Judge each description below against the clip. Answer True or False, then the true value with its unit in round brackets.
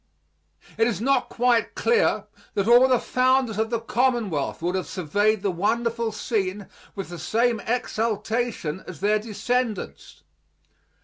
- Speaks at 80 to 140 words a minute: True (135 wpm)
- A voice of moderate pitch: False (225 Hz)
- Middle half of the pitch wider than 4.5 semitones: False (3.3 semitones)